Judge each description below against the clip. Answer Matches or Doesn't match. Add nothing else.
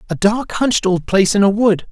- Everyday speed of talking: Doesn't match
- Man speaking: Matches